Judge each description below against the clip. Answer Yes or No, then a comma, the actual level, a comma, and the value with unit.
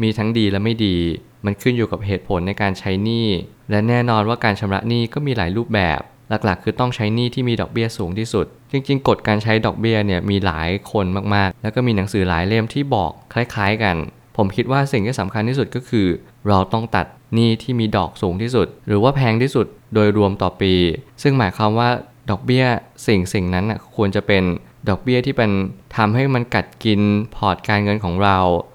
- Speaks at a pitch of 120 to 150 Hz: No, low, 105 Hz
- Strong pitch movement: No, average, 3.4 semitones